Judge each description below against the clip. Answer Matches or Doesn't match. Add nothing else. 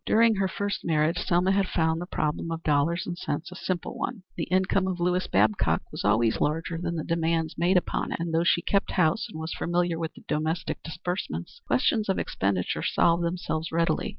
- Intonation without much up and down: Matches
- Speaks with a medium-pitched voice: Matches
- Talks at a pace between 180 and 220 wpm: Matches